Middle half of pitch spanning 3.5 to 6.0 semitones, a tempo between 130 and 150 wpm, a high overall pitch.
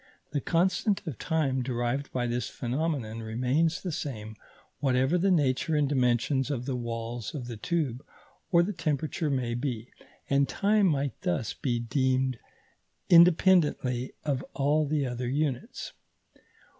No: average, 4.2 semitones; average, 140 wpm; low, 135 Hz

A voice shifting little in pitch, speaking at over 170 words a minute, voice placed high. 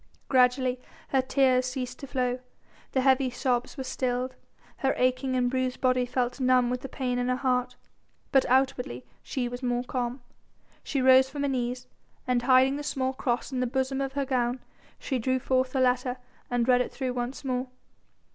Yes: narrow, 1.0 semitones; average, 185 wpm; very high, 255 Hz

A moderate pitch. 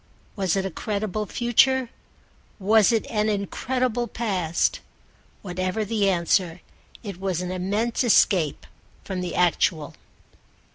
No: high, 200 Hz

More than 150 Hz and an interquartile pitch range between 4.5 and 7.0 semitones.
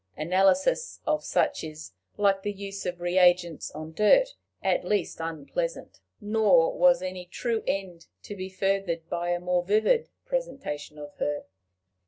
No: medium, 185 Hz; average, 3.6 semitones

